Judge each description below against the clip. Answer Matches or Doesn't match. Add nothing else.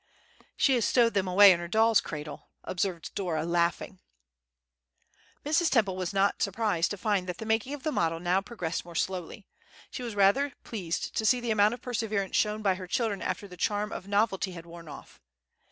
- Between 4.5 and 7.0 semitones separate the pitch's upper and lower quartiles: Doesn't match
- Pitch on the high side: Matches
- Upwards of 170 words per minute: Matches